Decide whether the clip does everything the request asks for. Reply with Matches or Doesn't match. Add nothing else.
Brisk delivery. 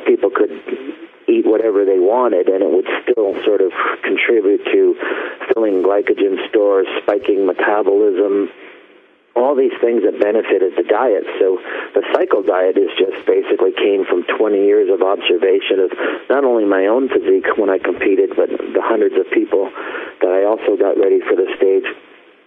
Doesn't match